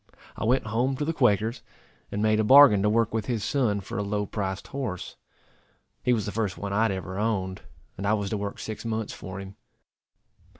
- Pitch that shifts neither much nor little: No, narrow, 2.3 semitones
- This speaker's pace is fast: Yes, fast, 215 wpm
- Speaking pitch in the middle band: No, low, 105 Hz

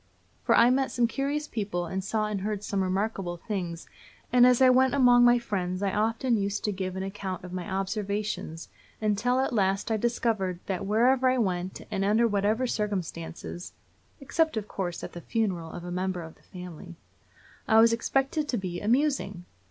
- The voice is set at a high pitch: Yes, high, 205 Hz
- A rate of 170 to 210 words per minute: Yes, average, 185 wpm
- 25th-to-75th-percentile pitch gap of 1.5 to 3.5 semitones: No, average, 4.3 semitones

